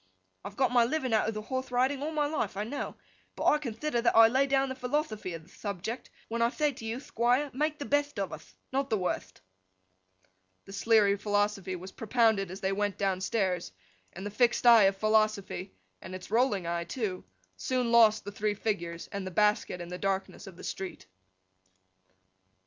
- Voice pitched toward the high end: Yes, high, 215 Hz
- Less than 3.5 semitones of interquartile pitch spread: No, average, 4.4 semitones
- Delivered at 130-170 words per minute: No, average, 190 wpm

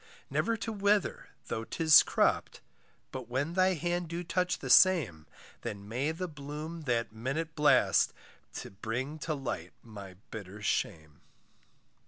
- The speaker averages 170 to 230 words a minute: No, average, 140 wpm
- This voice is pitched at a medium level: Yes, medium, 145 Hz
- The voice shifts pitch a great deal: Yes, wide, 7.2 semitones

